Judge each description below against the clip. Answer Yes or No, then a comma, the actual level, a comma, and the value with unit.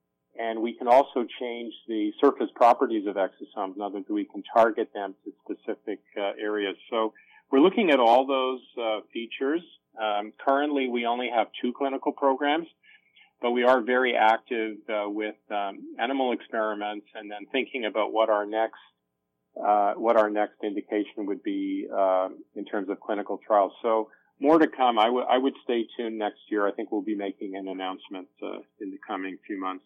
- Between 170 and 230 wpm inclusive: Yes, average, 185 wpm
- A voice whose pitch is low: Yes, low, 110 Hz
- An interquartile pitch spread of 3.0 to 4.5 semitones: Yes, average, 3.7 semitones